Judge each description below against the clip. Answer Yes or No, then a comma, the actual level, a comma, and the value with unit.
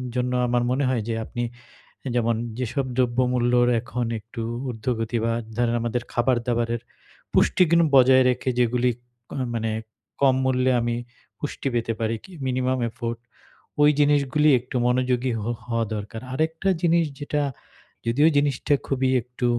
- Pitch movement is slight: Yes, narrow, 1.9 semitones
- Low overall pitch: Yes, low, 125 Hz